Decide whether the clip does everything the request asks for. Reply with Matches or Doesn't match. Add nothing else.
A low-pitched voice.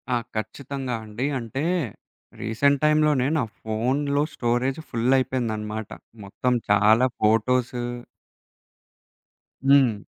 Matches